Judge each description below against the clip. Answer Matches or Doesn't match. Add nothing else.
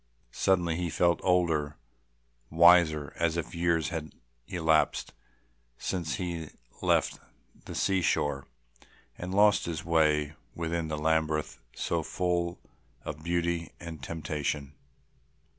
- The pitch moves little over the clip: Matches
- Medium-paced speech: Doesn't match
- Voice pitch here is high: Doesn't match